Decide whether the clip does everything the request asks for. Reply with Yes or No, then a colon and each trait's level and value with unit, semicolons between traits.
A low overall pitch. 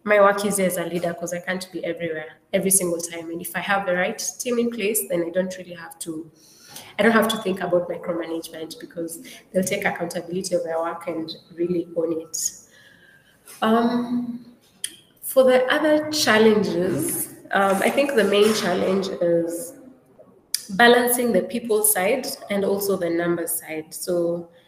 No: medium, 185 Hz